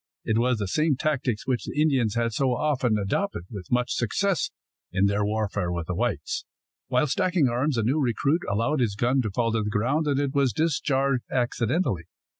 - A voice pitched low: Yes, low, 125 Hz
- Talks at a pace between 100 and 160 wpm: No, average, 195 wpm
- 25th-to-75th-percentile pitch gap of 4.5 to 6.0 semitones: Yes, average, 5.0 semitones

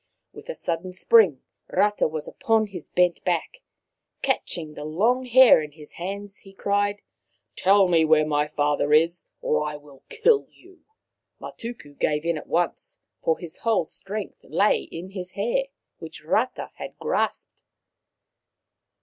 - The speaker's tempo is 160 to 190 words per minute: No, average, 150 wpm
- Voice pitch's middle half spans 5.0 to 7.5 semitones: Yes, average, 5.3 semitones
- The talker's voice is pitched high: No, medium, 180 Hz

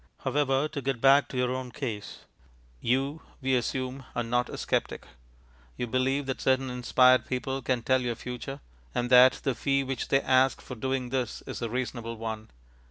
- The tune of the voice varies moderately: No, narrow, 1.5 semitones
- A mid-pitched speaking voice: No, low, 130 Hz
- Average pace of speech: Yes, average, 180 wpm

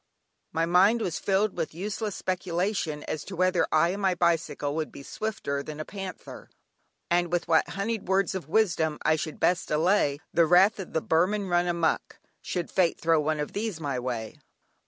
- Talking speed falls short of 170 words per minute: No, average, 190 wpm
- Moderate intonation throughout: Yes, average, 3.5 semitones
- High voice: No, medium, 175 Hz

